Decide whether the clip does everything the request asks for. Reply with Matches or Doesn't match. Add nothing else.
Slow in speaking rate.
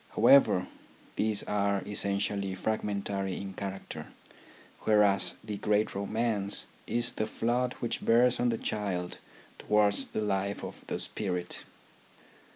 Matches